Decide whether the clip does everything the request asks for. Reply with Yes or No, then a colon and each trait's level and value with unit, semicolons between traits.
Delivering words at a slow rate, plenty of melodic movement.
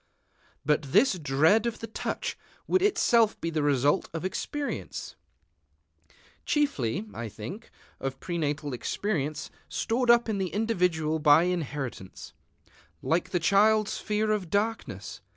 Yes: slow, 125 wpm; wide, 6.9 semitones